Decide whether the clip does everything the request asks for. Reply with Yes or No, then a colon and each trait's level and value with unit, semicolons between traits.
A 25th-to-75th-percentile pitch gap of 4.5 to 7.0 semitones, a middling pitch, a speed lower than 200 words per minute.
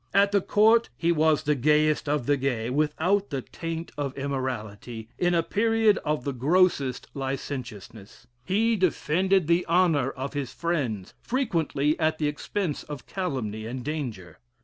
Yes: average, 5.2 semitones; medium, 150 Hz; average, 150 wpm